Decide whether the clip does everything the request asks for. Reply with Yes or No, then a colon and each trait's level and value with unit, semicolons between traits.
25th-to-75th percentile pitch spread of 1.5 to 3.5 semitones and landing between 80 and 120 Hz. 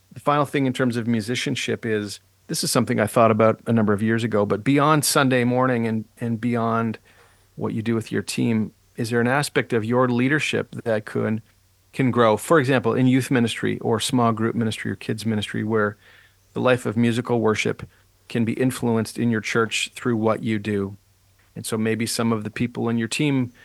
Yes: narrow, 2.4 semitones; low, 115 Hz